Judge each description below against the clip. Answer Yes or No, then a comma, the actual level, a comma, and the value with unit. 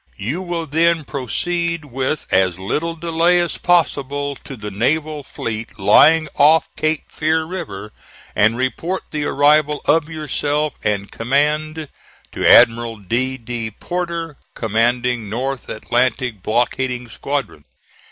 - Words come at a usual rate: No, slow, 125 wpm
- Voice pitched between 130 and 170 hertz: Yes, medium, 140 Hz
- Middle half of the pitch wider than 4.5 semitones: Yes, average, 5.3 semitones